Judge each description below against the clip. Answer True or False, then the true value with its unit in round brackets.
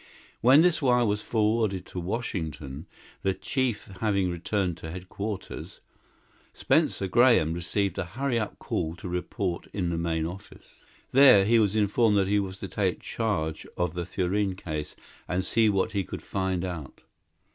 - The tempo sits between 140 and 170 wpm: True (160 wpm)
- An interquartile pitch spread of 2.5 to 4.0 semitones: True (3.5 semitones)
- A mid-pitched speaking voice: False (95 Hz)